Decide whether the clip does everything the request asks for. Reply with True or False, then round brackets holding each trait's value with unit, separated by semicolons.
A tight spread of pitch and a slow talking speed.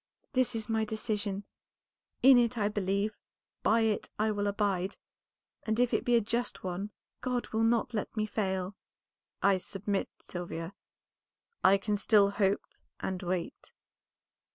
False (2.3 semitones; 145 wpm)